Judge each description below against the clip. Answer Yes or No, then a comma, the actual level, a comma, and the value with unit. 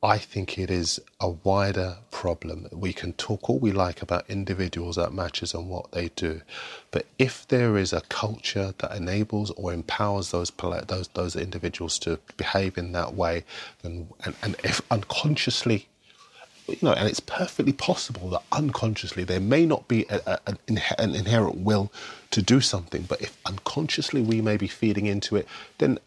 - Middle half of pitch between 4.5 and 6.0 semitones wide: No, average, 3.7 semitones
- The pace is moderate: Yes, average, 175 wpm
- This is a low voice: Yes, low, 100 Hz